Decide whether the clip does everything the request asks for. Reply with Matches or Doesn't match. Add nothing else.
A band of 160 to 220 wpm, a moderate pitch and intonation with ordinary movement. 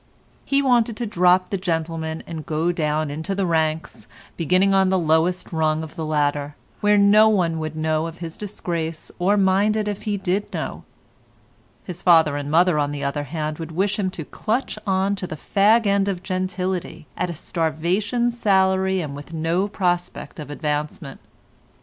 Matches